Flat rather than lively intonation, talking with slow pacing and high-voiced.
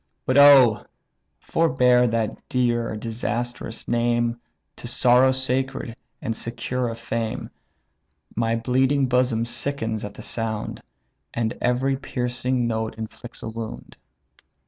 No: narrow, 1.9 semitones; slow, 115 wpm; low, 120 Hz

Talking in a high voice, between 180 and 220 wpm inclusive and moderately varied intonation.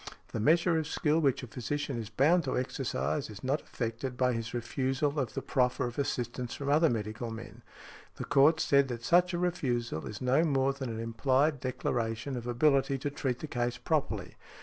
No: low, 130 Hz; average, 195 wpm; average, 3.6 semitones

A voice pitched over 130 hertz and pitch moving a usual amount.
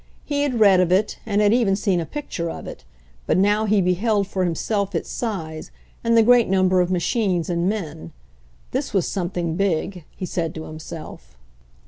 Yes: high, 190 Hz; average, 3.7 semitones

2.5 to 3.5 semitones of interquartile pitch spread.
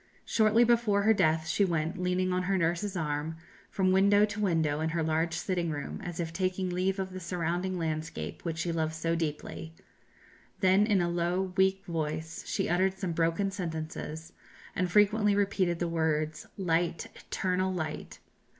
Yes: average, 2.8 semitones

